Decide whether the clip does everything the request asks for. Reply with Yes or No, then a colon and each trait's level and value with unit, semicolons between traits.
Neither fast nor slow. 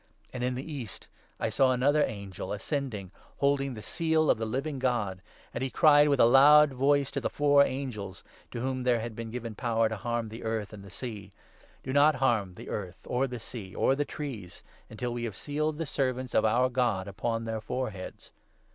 No: fast, 220 wpm